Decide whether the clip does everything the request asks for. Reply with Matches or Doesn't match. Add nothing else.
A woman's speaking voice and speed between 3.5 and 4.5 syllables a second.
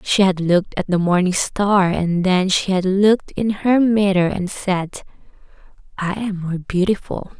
Matches